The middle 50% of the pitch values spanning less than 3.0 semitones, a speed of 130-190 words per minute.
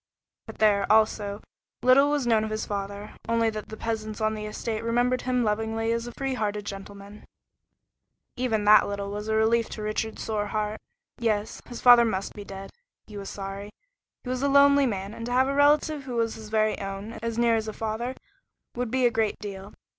No: narrow, 2.5 semitones; fast, 205 wpm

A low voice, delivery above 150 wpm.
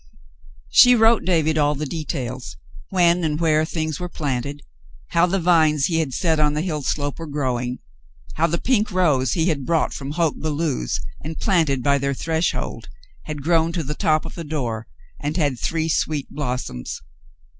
No: medium, 155 Hz; average, 185 wpm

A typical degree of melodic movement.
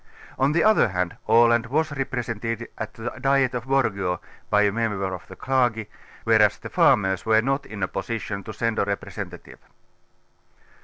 Yes: average, 4.3 semitones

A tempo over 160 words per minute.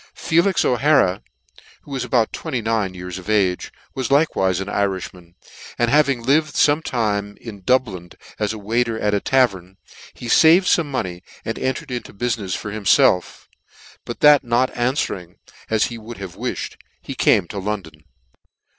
No: average, 155 wpm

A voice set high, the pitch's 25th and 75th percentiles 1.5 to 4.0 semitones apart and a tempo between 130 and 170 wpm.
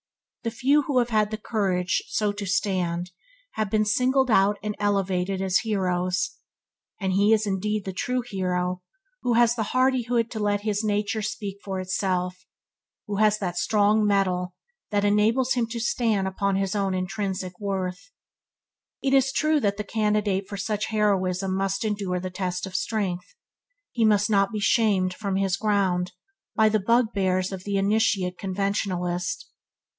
Yes: high, 200 Hz; narrow, 2.5 semitones; average, 160 wpm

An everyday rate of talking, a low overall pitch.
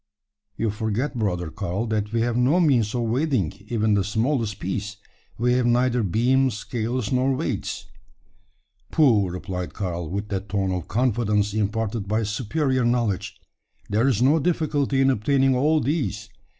Yes: average, 150 wpm; low, 115 Hz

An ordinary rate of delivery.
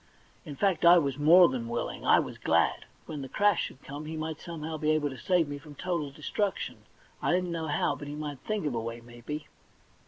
No: fast, 225 wpm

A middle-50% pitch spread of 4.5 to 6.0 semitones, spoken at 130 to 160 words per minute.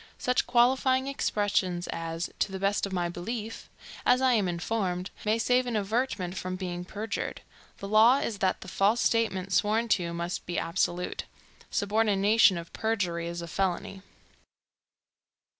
No: average, 4.1 semitones; average, 150 wpm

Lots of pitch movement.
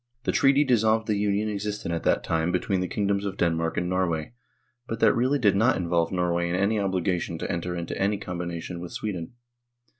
No: average, 3.4 semitones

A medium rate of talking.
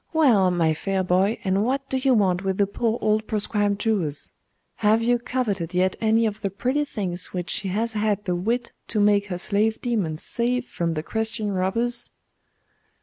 Yes: average, 185 wpm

